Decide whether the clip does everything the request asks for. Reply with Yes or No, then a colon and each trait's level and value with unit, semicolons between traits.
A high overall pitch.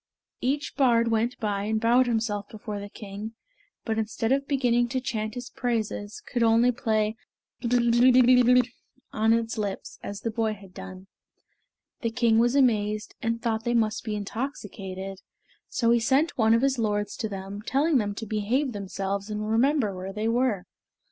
Yes: high, 225 Hz